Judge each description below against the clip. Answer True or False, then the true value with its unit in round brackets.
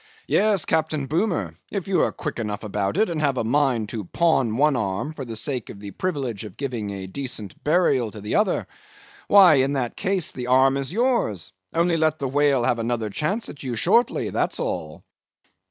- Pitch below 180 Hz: True (135 Hz)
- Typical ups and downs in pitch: False (6.3 semitones)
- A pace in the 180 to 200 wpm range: True (195 wpm)